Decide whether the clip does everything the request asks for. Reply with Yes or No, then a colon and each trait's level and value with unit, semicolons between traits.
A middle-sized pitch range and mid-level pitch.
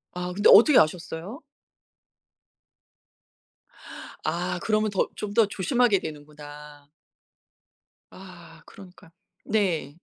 Yes: average, 4.8 semitones; medium, 180 Hz